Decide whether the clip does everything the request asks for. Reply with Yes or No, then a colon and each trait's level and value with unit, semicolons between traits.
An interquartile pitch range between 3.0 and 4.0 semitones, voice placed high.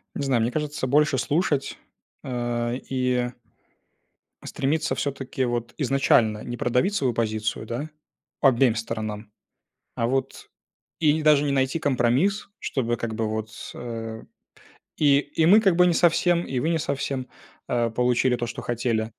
No: average, 3.7 semitones; low, 125 Hz